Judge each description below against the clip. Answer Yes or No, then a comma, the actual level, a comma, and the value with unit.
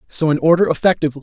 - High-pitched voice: No, medium, 155 Hz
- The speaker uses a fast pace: No, average, 195 wpm